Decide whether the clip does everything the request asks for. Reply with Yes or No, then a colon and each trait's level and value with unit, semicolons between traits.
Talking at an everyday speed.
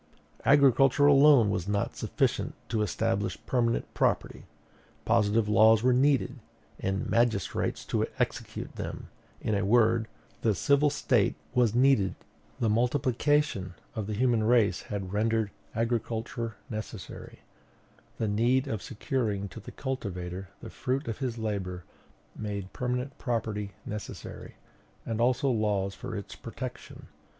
No: slow, 125 wpm